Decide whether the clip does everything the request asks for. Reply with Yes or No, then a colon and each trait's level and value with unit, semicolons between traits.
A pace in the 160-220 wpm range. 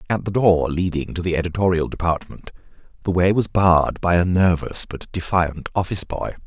Yes: average, 175 wpm